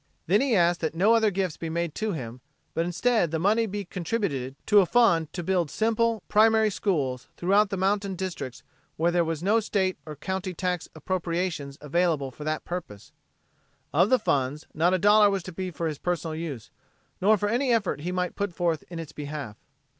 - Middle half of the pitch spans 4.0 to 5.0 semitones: Yes, average, 4.3 semitones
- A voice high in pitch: No, medium, 180 Hz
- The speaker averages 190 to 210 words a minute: Yes, average, 200 wpm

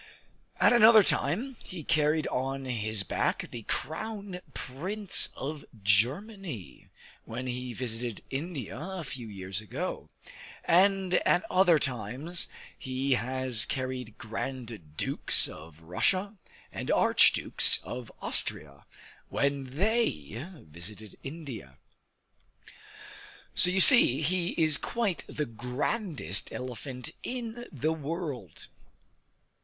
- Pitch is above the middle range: No, low, 135 Hz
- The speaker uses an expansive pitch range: Yes, wide, 7.7 semitones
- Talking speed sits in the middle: No, slow, 105 wpm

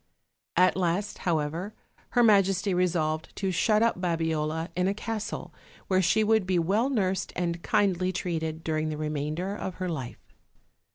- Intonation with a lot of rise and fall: No, average, 3.3 semitones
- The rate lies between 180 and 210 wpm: No, average, 155 wpm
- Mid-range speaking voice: Yes, medium, 180 Hz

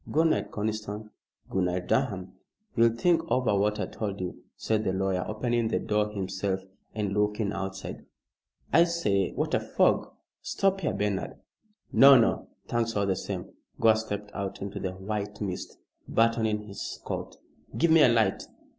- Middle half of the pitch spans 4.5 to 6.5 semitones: No, average, 2.9 semitones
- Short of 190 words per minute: Yes, average, 165 wpm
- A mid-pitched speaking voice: No, low, 105 Hz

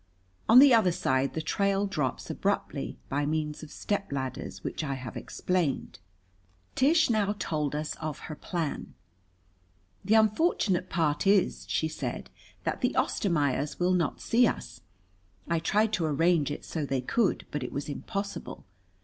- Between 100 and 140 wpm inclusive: No, average, 150 wpm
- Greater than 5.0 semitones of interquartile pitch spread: Yes, wide, 5.6 semitones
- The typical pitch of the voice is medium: Yes, medium, 165 Hz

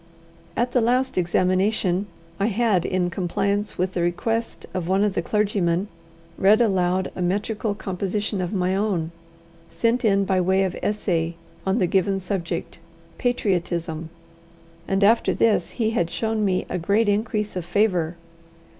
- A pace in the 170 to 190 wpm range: No, average, 150 wpm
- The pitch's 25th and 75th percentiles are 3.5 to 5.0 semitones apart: No, average, 3.0 semitones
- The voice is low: No, high, 195 Hz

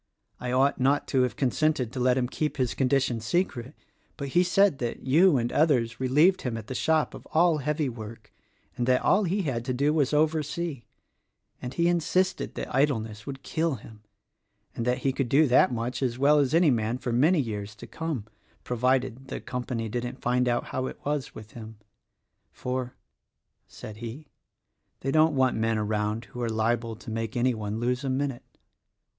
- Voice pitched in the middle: No, low, 130 Hz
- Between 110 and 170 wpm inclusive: No, average, 195 wpm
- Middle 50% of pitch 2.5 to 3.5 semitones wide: No, average, 4.1 semitones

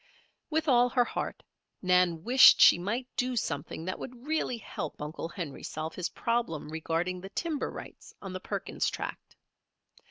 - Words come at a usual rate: Yes, average, 160 wpm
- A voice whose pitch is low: No, medium, 185 Hz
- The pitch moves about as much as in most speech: No, wide, 6.9 semitones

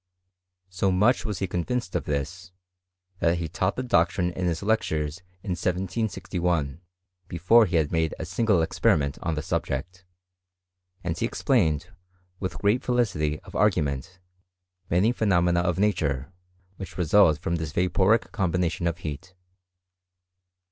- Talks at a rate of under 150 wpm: Yes, average, 140 wpm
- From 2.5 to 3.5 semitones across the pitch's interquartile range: Yes, average, 3.1 semitones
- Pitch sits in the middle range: No, very low, 90 Hz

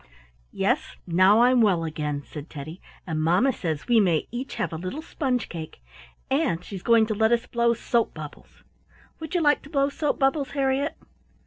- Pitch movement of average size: No, wide, 8.1 semitones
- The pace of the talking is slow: No, average, 185 wpm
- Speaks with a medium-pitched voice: No, high, 225 Hz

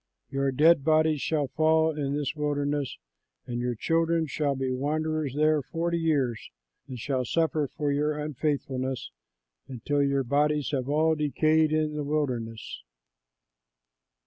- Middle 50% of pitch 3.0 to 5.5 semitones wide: No, narrow, 2.4 semitones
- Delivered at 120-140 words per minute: Yes, slow, 135 wpm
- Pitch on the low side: No, medium, 145 Hz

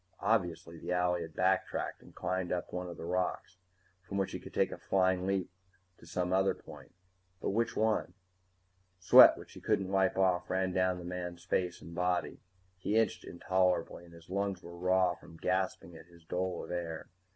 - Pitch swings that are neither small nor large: No, narrow, 1.3 semitones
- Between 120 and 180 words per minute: No, average, 190 wpm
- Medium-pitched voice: No, very low, 90 Hz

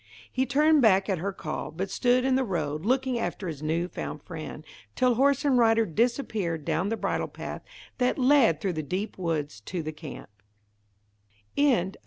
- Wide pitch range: Yes, wide, 8.2 semitones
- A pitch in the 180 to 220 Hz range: Yes, medium, 185 Hz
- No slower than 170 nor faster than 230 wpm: Yes, average, 180 wpm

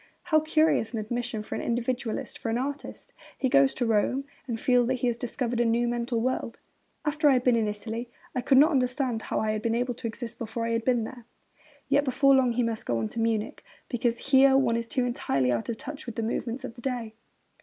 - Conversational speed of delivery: No, fast, 240 wpm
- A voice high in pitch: Yes, high, 240 Hz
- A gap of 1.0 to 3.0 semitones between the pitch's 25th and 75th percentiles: Yes, narrow, 2.4 semitones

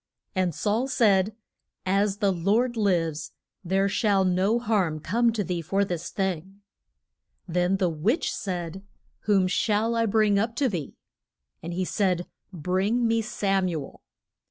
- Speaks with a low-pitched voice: No, high, 195 Hz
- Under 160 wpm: Yes, average, 150 wpm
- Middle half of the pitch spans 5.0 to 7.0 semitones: No, average, 3.2 semitones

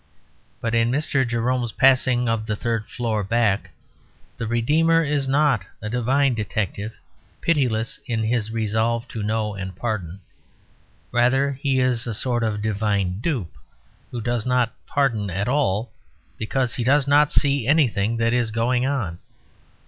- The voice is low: Yes, low, 115 Hz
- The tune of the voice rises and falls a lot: No, average, 3.3 semitones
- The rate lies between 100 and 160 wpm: Yes, average, 150 wpm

